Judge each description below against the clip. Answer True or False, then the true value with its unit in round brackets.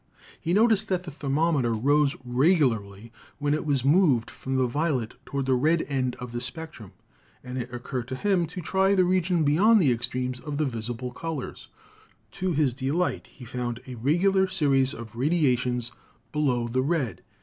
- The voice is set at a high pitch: False (140 Hz)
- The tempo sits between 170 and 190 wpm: True (175 wpm)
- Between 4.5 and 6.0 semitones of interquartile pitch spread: True (5.1 semitones)